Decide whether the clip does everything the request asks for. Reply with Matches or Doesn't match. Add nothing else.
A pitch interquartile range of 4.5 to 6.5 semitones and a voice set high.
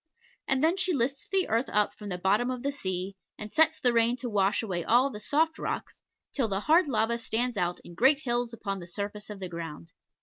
Matches